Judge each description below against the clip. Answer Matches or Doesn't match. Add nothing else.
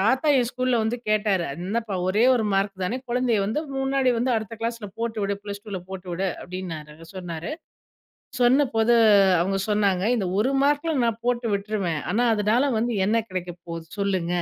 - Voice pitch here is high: Matches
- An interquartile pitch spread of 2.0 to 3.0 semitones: Doesn't match